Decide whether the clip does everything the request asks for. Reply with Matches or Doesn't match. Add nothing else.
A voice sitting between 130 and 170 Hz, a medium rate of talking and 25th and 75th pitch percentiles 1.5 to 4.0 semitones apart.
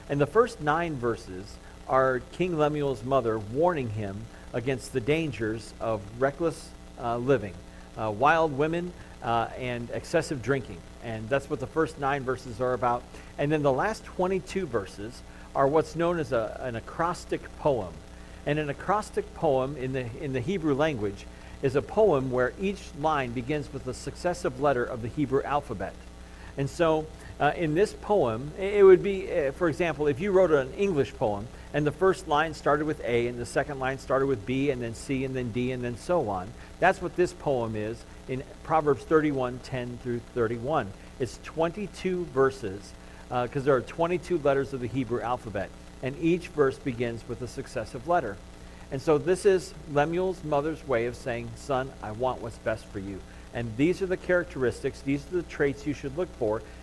Doesn't match